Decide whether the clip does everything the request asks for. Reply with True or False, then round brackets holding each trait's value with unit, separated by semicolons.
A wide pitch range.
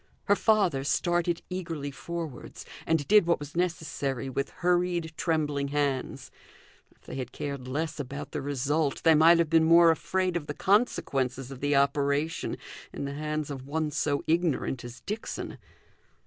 False (3.4 semitones)